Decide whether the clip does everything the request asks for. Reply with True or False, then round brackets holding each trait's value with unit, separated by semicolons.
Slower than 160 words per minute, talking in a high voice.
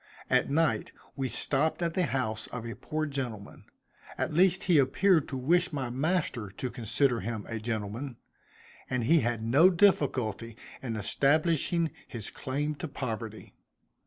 False (150 wpm; 135 Hz)